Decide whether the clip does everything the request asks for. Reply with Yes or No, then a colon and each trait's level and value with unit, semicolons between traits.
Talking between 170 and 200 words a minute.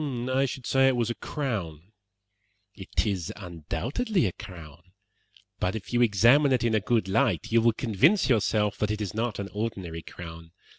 Yes: average, 180 wpm